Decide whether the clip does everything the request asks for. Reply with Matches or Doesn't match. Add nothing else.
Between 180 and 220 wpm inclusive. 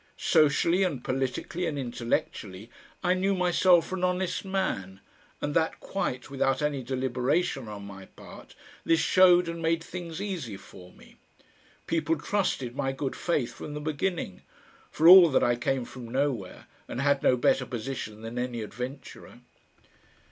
Doesn't match